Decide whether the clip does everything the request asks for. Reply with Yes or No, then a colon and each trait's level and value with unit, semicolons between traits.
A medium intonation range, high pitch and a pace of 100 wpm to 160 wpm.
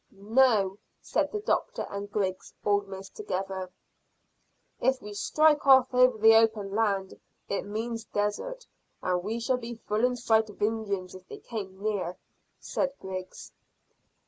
Yes: average, 3.6 semitones; high, 210 Hz; average, 145 wpm